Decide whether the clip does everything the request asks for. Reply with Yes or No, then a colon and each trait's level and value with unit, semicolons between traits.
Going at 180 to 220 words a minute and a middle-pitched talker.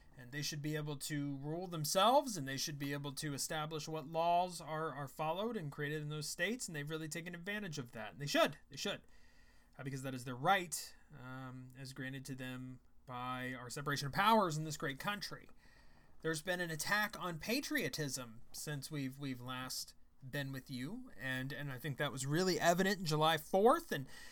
Yes: average, 200 wpm; medium, 150 Hz